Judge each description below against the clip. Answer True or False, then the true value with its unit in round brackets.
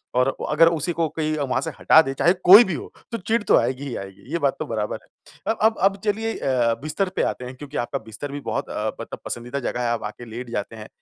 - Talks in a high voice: False (140 Hz)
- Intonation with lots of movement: True (5.7 semitones)